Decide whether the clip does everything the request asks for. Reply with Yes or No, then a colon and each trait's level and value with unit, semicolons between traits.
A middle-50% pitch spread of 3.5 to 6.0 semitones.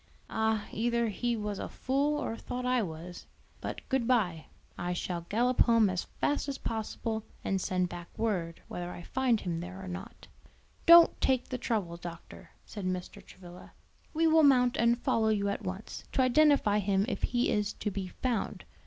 Yes: average, 5.2 semitones